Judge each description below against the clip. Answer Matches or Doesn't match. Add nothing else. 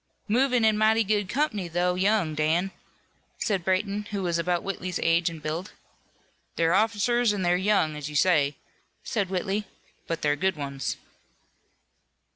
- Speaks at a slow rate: Doesn't match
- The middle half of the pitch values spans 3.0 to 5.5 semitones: Matches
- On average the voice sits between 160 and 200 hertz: Matches